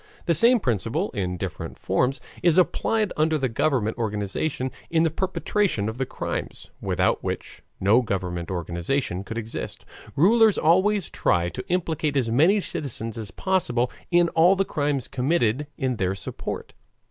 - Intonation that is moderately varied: No, wide, 7.7 semitones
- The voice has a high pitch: No, low, 135 Hz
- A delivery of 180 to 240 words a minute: No, average, 150 wpm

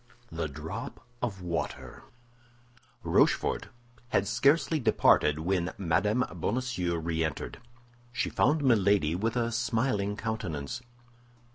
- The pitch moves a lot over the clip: Yes, wide, 5.9 semitones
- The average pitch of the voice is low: Yes, low, 100 Hz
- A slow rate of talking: Yes, slow, 105 wpm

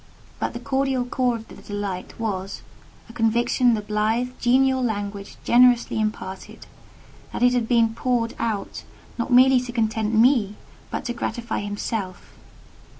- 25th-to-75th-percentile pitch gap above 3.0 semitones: No, average, 2.7 semitones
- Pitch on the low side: No, high, 230 Hz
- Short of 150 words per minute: Yes, average, 140 wpm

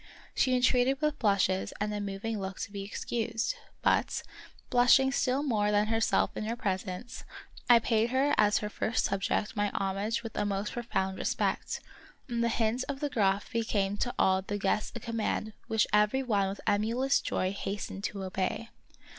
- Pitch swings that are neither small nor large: Yes, average, 3.2 semitones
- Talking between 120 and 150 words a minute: No, average, 180 wpm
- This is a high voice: Yes, high, 215 Hz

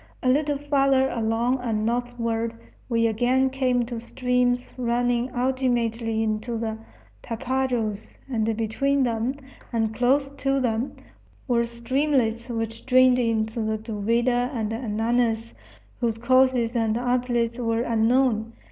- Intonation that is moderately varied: No, narrow, 2.1 semitones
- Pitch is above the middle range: Yes, high, 240 Hz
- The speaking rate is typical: No, slow, 120 wpm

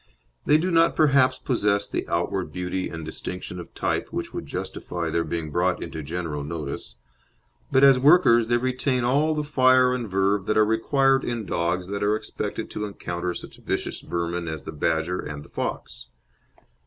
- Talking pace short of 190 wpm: Yes, average, 180 wpm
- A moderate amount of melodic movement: No, wide, 7.0 semitones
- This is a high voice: No, low, 100 Hz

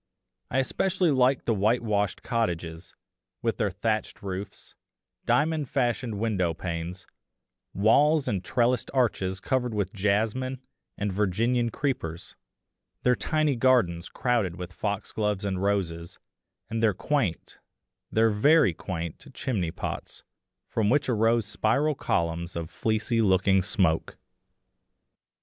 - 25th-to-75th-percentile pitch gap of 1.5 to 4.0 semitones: No, average, 4.8 semitones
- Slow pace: Yes, slow, 115 wpm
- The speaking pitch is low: Yes, low, 105 Hz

